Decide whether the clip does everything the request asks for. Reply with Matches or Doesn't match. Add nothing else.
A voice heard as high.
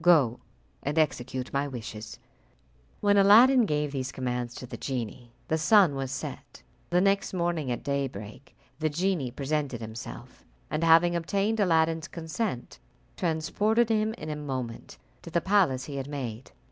Doesn't match